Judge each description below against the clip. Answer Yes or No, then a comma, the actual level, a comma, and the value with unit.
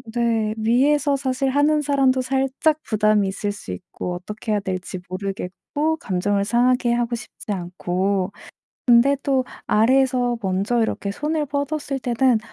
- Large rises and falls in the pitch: No, average, 5.0 semitones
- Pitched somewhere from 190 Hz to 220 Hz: No, high, 240 Hz